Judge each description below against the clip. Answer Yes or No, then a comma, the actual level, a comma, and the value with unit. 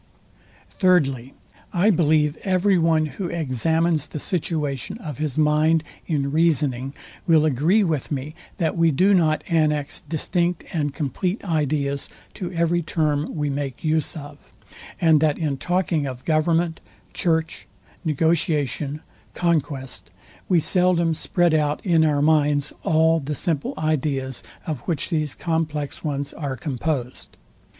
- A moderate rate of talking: No, slow, 130 wpm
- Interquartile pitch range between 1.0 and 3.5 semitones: Yes, narrow, 2.5 semitones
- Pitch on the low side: No, medium, 155 Hz